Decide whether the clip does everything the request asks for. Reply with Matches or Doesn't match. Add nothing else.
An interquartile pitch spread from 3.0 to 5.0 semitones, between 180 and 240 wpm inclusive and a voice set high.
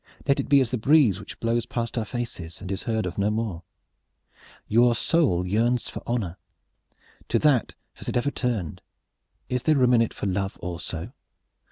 Doesn't match